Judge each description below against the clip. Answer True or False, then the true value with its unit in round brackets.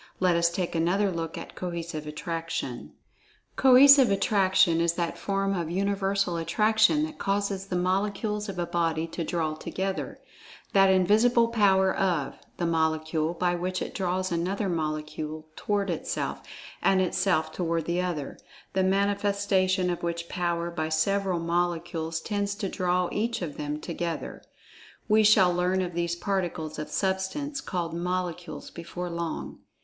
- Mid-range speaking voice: True (180 Hz)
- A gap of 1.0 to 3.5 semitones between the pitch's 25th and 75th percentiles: True (2.7 semitones)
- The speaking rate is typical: True (145 wpm)